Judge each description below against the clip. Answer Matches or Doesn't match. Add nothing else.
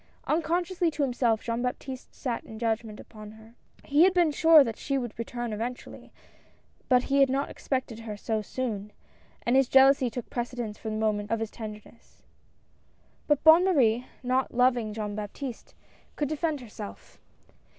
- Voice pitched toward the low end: Doesn't match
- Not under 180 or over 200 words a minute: Doesn't match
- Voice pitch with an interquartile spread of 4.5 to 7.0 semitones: Doesn't match